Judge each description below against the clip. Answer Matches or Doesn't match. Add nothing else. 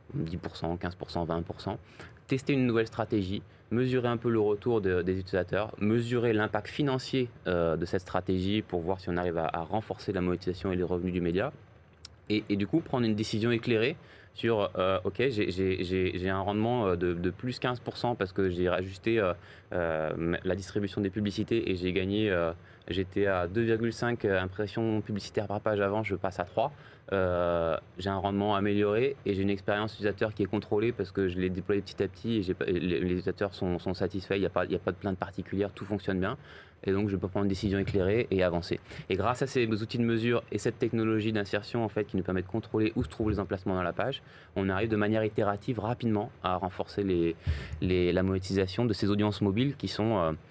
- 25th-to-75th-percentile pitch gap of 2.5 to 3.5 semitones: Matches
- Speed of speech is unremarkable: Matches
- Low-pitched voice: Matches